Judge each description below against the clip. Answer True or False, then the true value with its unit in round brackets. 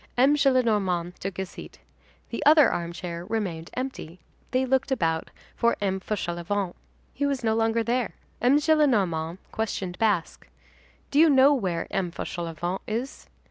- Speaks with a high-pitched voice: True (215 Hz)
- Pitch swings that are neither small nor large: False (6.8 semitones)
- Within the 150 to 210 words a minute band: False (140 wpm)